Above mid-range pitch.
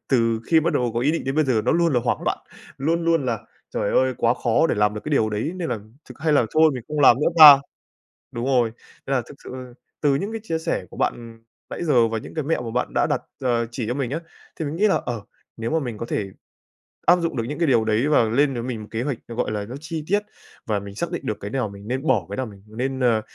No: low, 125 Hz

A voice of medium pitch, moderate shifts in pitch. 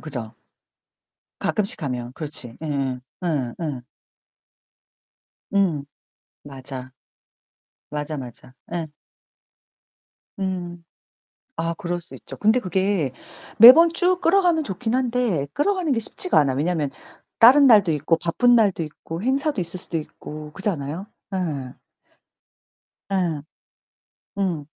No: medium, 175 Hz; wide, 7.1 semitones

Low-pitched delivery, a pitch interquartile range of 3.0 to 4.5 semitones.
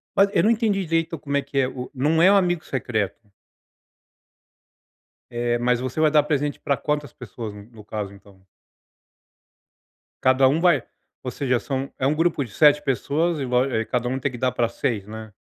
Yes: low, 130 Hz; average, 4.2 semitones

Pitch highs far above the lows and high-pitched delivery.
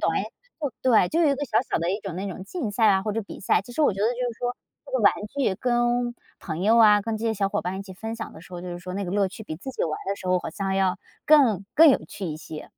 No: average, 4.4 semitones; high, 205 Hz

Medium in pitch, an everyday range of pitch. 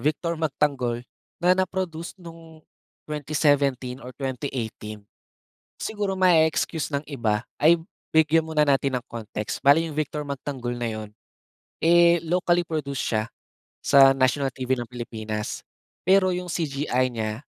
Yes: medium, 145 Hz; average, 4.7 semitones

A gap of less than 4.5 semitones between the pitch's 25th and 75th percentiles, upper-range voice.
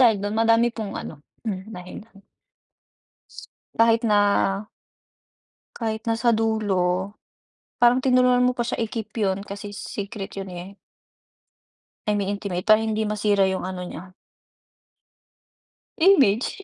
Yes: average, 2.7 semitones; high, 210 Hz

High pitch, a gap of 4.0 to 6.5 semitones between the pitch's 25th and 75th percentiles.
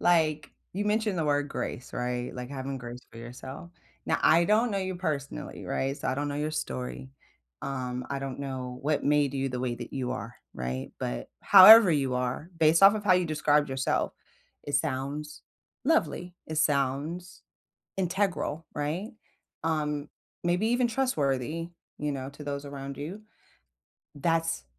No: medium, 145 Hz; average, 4.4 semitones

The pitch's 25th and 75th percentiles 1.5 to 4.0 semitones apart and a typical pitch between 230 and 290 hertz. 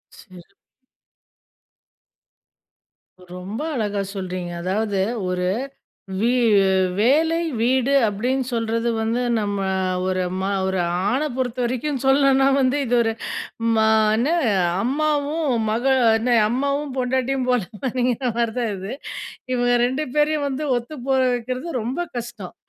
Yes: average, 3.5 semitones; high, 245 Hz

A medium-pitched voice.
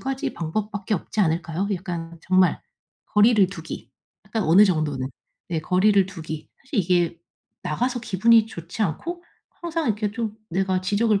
No: high, 195 Hz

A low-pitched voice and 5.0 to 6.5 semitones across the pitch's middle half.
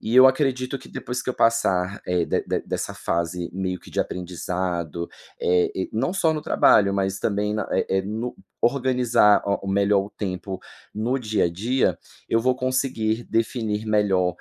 Yes: low, 105 Hz; average, 5.3 semitones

